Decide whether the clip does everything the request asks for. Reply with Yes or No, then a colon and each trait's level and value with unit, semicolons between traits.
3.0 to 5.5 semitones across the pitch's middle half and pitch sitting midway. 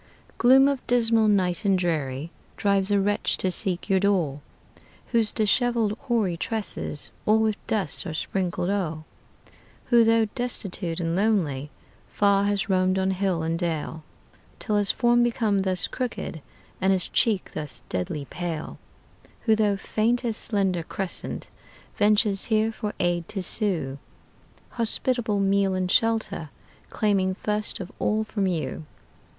No: average, 3.7 semitones; high, 200 Hz